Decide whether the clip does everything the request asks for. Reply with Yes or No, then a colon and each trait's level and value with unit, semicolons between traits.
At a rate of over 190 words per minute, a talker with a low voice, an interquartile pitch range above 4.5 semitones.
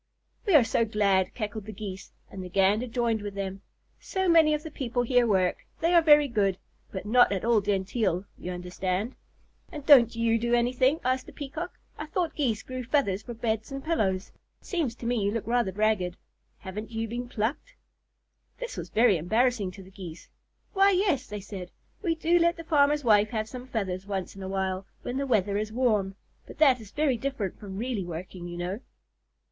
No: average, 200 wpm; high, 225 Hz; average, 5.3 semitones